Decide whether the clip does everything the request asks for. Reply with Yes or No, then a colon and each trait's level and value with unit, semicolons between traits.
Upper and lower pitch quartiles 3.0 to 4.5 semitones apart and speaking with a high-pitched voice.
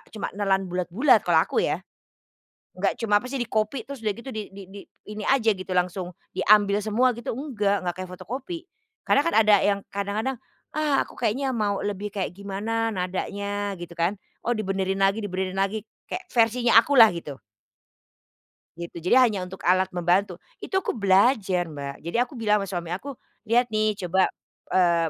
Yes: average, 3.4 semitones; high, 205 Hz